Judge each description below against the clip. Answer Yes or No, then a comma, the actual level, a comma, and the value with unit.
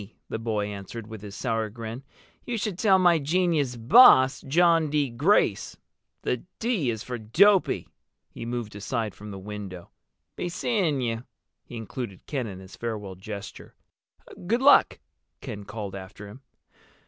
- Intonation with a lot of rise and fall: Yes, wide, 7.5 semitones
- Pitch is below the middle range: Yes, low, 115 Hz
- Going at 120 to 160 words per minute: Yes, average, 150 wpm